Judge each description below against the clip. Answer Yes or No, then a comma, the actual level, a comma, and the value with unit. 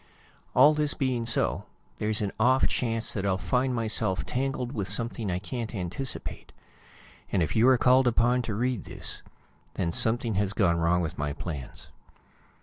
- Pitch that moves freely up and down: No, average, 4.9 semitones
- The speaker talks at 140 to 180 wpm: Yes, average, 165 wpm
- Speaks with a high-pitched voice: No, low, 110 Hz